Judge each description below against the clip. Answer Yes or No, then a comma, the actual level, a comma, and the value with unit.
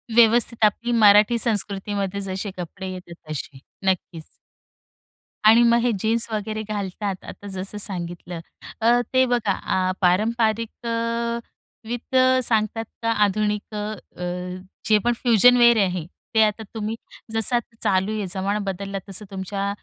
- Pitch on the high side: Yes, high, 210 Hz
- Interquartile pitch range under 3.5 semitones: Yes, average, 3.1 semitones